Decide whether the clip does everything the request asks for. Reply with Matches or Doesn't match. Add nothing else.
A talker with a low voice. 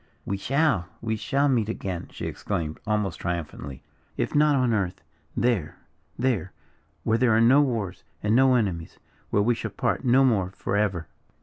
Matches